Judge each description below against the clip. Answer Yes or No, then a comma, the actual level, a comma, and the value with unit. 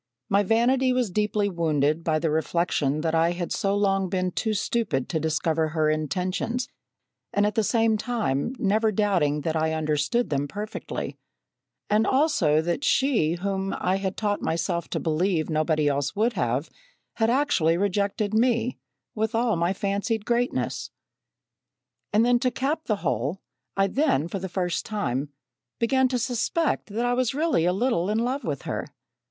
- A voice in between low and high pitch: No, high, 195 Hz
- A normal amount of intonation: No, wide, 6.2 semitones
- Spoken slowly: No, average, 165 wpm